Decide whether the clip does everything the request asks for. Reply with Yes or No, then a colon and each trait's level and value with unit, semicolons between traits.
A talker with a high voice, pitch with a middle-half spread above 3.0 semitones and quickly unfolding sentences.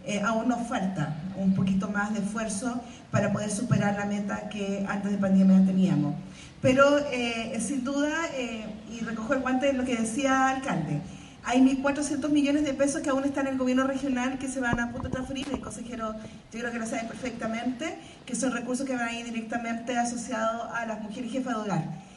Yes: high, 235 Hz; average, 4.2 semitones; fast, 210 wpm